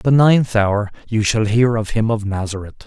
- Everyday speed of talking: No, fast, 230 wpm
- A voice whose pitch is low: Yes, low, 110 Hz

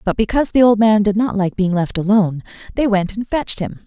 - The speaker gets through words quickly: Yes, fast, 250 wpm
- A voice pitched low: No, high, 210 Hz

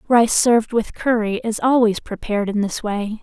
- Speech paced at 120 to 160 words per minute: No, average, 185 wpm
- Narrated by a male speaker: No, female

